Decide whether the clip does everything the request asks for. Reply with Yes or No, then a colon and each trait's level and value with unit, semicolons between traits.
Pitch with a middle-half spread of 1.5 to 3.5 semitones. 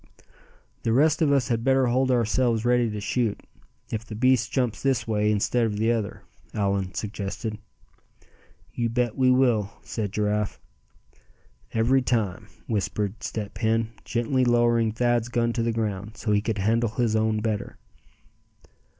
Yes: narrow, 2.4 semitones